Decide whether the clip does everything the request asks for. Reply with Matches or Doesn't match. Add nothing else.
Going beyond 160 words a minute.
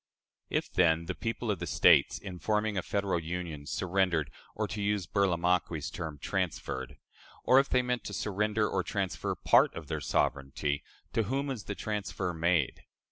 Matches